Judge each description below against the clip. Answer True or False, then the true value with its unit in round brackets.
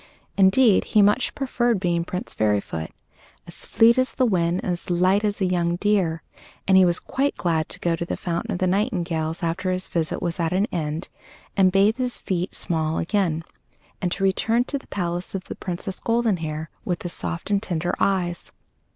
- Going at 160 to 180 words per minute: False (195 wpm)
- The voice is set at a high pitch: False (180 Hz)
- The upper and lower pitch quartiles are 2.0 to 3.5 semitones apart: True (3.1 semitones)